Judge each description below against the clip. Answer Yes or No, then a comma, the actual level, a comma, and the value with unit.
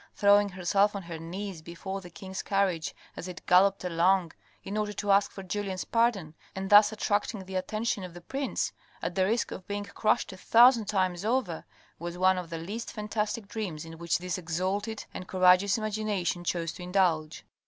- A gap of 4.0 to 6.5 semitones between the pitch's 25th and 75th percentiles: No, narrow, 2.6 semitones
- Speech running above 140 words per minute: Yes, average, 185 wpm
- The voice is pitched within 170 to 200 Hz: Yes, high, 190 Hz